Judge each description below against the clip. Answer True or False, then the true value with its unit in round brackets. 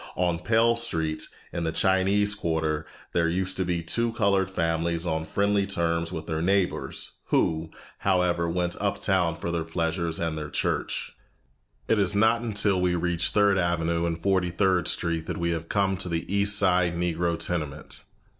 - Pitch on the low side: True (85 Hz)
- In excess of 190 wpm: False (165 wpm)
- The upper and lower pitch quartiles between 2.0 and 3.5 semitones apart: True (2.9 semitones)